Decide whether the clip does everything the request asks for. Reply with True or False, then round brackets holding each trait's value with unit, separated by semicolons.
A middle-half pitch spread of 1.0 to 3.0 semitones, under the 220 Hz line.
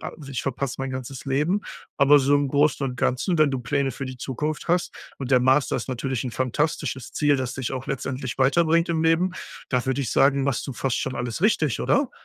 True (2.5 semitones; 135 Hz)